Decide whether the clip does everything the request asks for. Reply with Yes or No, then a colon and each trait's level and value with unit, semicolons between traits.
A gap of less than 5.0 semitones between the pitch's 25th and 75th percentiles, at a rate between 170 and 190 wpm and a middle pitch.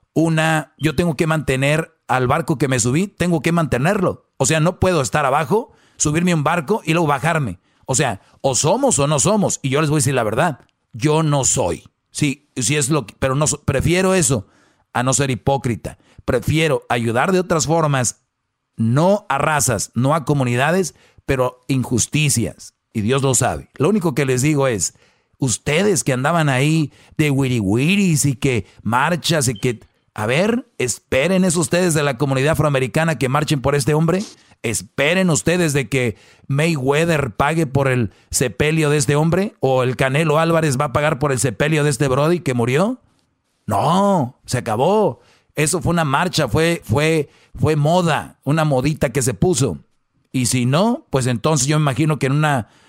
Yes: average, 3.9 semitones; average, 180 wpm; medium, 145 Hz